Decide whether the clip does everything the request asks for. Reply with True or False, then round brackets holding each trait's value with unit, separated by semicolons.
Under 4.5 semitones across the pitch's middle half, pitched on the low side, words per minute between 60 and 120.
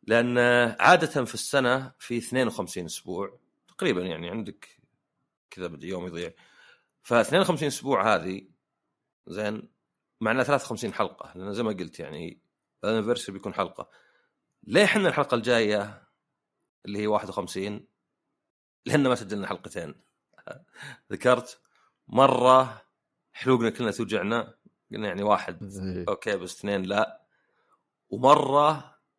False (5.1 semitones; 120 Hz; 110 wpm)